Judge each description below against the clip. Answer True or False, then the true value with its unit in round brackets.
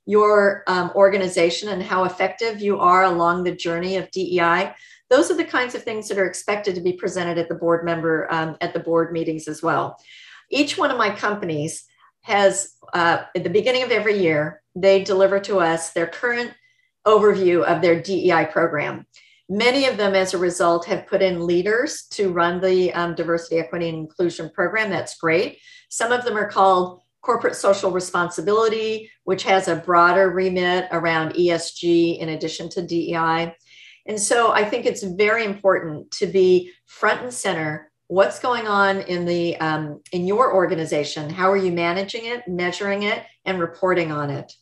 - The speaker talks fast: False (180 wpm)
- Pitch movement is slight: False (3.3 semitones)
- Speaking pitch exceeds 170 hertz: True (185 Hz)